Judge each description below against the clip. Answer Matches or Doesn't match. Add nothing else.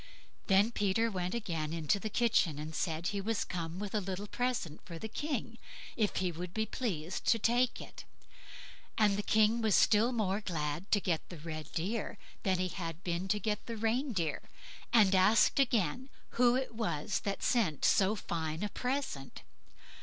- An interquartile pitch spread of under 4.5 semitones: Doesn't match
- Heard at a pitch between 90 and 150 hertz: Doesn't match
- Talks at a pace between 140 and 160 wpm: Doesn't match